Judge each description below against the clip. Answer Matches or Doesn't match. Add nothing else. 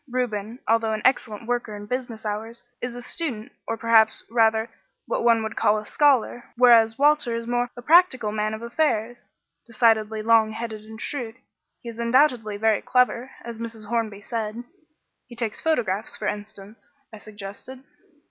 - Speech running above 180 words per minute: Doesn't match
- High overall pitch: Matches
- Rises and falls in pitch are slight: Matches